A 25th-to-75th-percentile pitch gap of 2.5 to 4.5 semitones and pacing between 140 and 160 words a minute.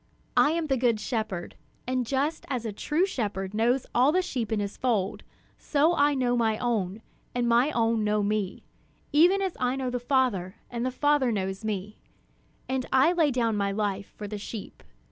No: average, 4.2 semitones; average, 190 wpm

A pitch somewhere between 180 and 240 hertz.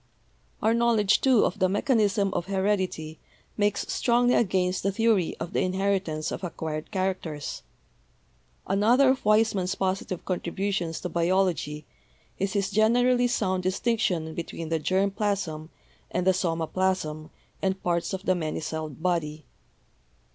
Yes: high, 190 Hz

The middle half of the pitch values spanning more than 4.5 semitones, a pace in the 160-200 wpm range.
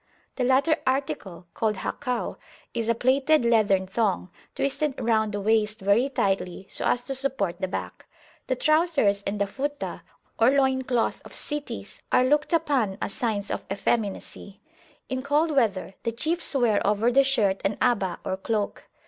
Yes: average, 5.1 semitones; average, 165 wpm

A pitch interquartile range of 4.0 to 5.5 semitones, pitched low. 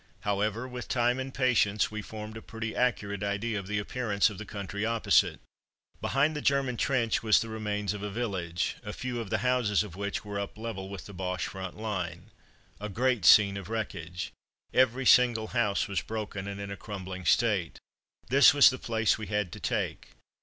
No: average, 2.9 semitones; low, 105 Hz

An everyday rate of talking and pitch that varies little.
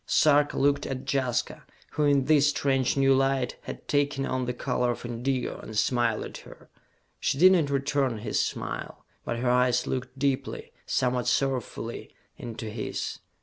Yes: average, 160 wpm; narrow, 2.2 semitones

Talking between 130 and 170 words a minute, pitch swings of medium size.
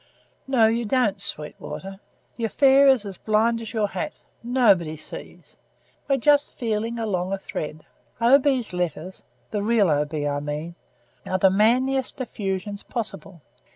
Yes: average, 150 wpm; average, 4.7 semitones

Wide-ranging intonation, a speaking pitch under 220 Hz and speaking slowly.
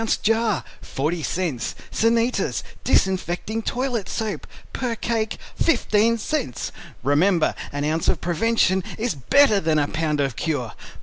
Yes: wide, 6.7 semitones; high, 190 Hz; slow, 125 wpm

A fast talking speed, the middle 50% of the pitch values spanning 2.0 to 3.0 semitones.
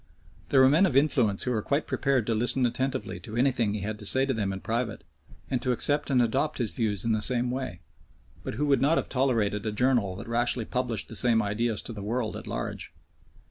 No: fast, 230 wpm; average, 3.4 semitones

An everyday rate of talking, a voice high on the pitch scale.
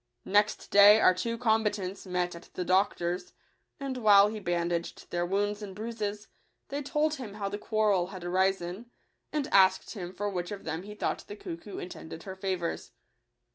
Yes: average, 175 wpm; high, 200 Hz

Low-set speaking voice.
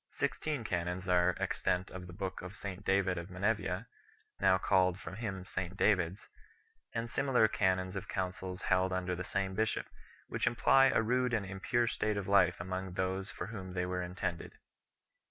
Yes: very low, 95 Hz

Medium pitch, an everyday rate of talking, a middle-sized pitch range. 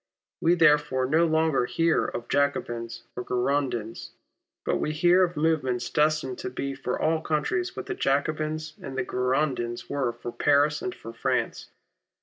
Yes: medium, 145 Hz; average, 155 wpm; average, 3.9 semitones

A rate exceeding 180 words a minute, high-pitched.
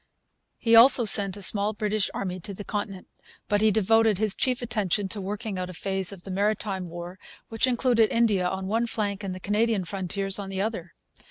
Yes: average, 200 wpm; high, 205 Hz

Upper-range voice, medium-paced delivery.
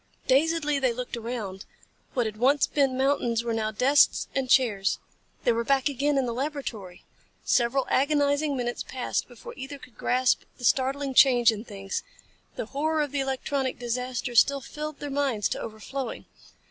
Yes: very high, 260 Hz; average, 165 wpm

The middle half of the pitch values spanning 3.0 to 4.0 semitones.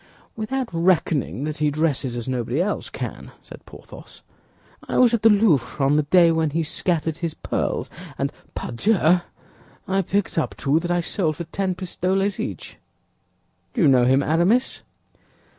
No: average, 4.5 semitones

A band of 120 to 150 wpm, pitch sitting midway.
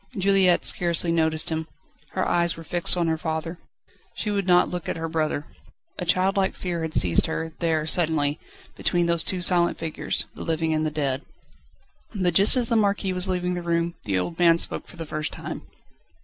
No: average, 195 wpm; medium, 170 Hz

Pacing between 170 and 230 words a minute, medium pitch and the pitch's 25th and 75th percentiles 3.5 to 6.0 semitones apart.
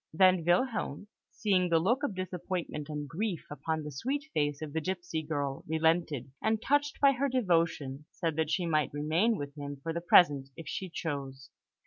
Yes: average, 180 wpm; medium, 165 Hz; average, 4.2 semitones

